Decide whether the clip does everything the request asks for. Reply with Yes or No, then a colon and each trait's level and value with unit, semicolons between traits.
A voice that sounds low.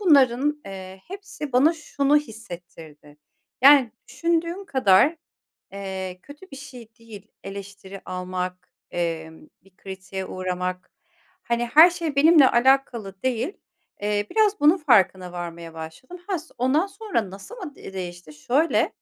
No: high, 230 Hz